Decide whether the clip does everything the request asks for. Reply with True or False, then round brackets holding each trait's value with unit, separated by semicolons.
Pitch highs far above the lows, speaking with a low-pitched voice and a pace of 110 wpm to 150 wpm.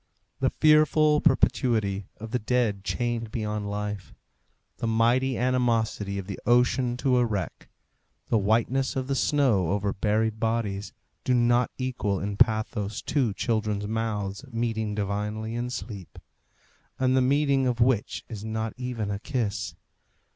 False (3.3 semitones; 115 Hz; 140 wpm)